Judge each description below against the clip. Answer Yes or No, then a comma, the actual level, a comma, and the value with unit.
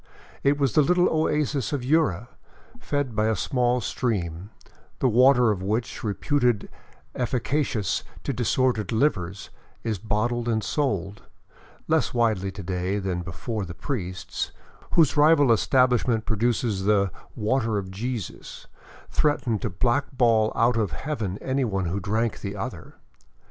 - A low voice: Yes, low, 115 Hz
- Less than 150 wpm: Yes, average, 140 wpm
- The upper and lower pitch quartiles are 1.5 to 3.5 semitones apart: No, average, 4.6 semitones